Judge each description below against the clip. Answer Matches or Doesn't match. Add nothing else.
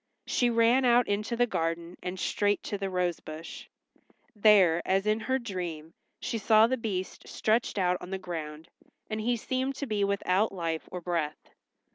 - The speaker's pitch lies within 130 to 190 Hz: Doesn't match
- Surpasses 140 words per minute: Matches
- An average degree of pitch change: Matches